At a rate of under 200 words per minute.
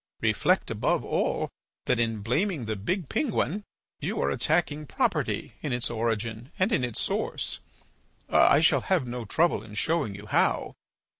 Yes: average, 155 wpm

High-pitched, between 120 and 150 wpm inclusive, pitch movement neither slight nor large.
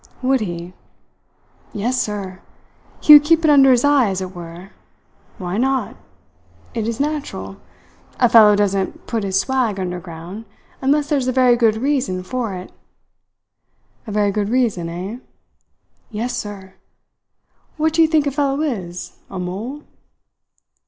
No: high, 225 Hz; average, 145 wpm; wide, 5.9 semitones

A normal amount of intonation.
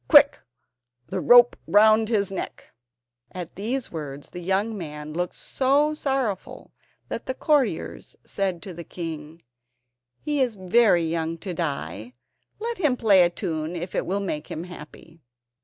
No: wide, 6.5 semitones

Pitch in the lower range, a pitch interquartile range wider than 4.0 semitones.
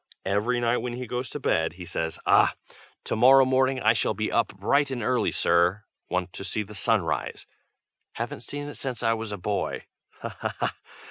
Yes: low, 115 Hz; average, 4.5 semitones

